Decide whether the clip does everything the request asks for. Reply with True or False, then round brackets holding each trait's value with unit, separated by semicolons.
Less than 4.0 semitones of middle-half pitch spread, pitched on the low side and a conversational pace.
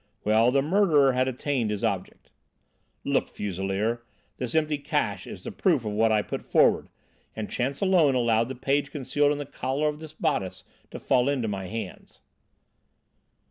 False (4.7 semitones; 125 Hz; 170 wpm)